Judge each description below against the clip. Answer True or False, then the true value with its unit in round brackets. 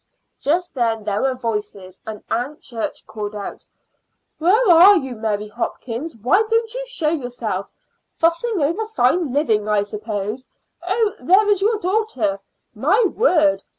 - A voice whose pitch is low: False (265 Hz)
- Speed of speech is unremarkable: True (145 wpm)